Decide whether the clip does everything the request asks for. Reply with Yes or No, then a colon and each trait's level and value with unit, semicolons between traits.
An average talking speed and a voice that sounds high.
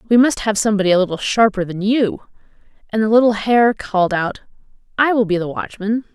Yes: average, 195 wpm; high, 215 Hz